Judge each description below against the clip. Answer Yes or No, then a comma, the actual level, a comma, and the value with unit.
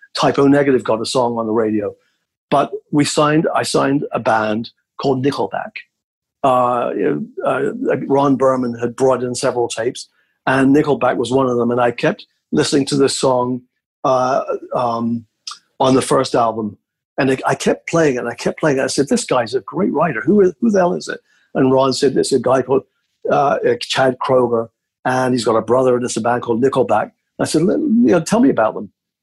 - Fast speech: Yes, fast, 210 wpm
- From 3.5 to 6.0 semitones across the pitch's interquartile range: No, average, 3.0 semitones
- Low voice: Yes, low, 130 Hz